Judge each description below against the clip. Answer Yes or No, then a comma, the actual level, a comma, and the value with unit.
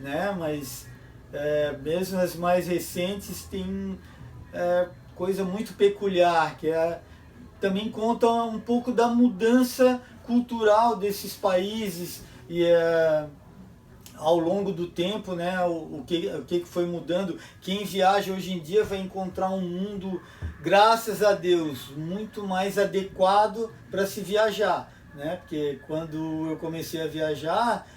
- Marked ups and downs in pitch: No, average, 3.9 semitones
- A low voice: No, medium, 185 Hz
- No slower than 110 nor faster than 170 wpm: Yes, average, 135 wpm